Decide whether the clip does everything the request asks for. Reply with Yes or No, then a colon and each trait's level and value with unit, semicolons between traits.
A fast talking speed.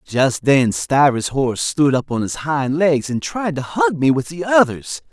Yes: fast, 210 wpm